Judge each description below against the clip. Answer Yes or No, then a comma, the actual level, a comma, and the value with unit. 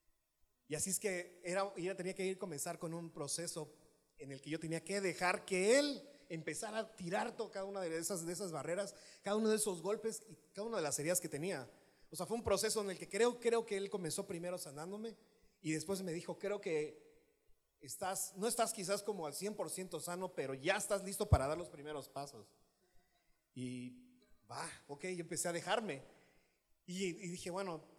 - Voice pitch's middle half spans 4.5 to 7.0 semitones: No, average, 4.0 semitones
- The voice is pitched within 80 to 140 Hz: No, medium, 185 Hz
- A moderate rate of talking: No, fast, 205 wpm